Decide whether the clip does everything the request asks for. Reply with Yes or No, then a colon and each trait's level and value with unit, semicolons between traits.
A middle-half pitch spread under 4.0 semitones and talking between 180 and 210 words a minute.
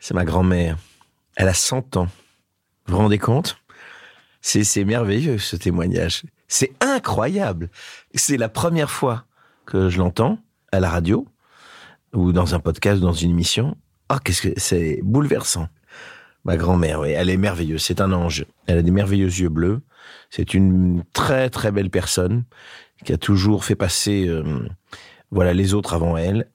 No: average, 3.1 semitones; average, 165 wpm